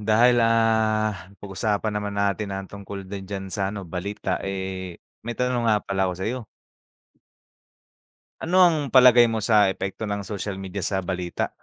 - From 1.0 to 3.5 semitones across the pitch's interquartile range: Yes, narrow, 2.5 semitones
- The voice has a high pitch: No, low, 100 Hz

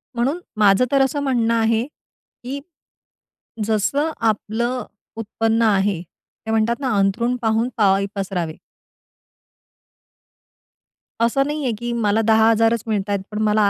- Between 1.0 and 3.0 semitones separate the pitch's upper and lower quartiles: Yes, narrow, 2.6 semitones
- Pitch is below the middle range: No, high, 225 Hz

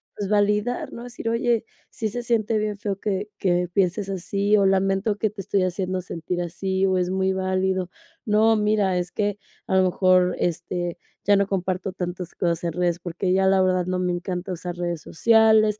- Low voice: No, high, 190 Hz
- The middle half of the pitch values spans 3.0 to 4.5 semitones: No, narrow, 2.5 semitones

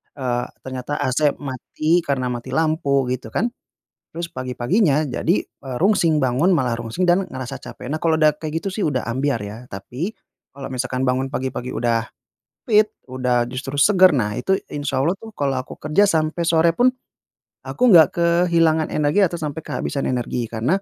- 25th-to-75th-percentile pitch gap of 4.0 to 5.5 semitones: Yes, average, 4.7 semitones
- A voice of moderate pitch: Yes, medium, 145 Hz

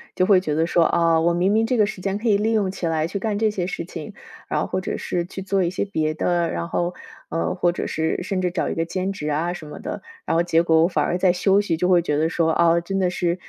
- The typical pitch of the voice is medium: Yes, medium, 175 Hz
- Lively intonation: No, average, 2.7 semitones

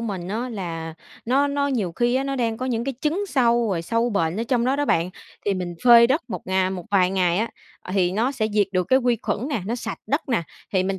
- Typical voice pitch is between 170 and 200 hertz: No, high, 225 Hz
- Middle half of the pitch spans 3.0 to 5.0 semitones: No, wide, 5.4 semitones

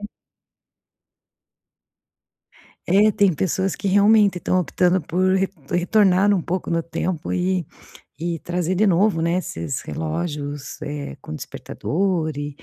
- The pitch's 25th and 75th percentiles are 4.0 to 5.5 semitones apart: No, average, 3.1 semitones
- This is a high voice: No, medium, 180 Hz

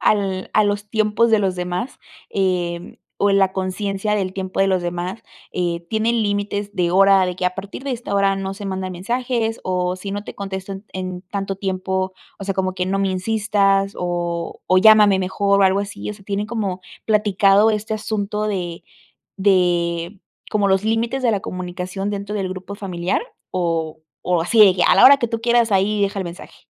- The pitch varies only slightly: Yes, narrow, 2.1 semitones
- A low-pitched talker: No, high, 195 Hz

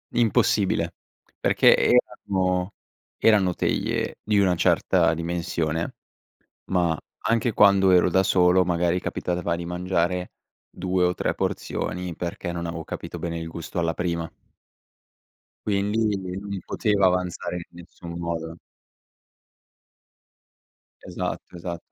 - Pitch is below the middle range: Yes, very low, 90 Hz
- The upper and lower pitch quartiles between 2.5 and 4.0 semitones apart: No, narrow, 1.9 semitones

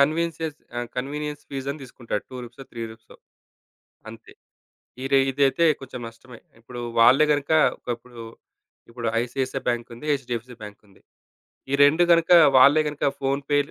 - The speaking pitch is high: No, low, 135 Hz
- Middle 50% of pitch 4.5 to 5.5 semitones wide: No, average, 3.3 semitones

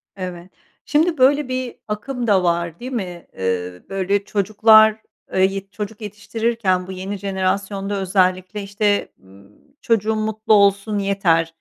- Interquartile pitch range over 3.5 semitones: No, average, 2.8 semitones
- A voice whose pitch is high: Yes, high, 200 Hz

